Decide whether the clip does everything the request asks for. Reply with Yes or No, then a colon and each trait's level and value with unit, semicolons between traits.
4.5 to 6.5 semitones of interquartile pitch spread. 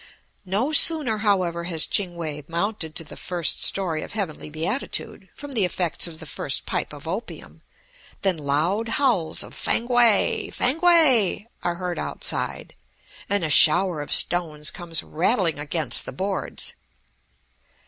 Yes: average, 5.2 semitones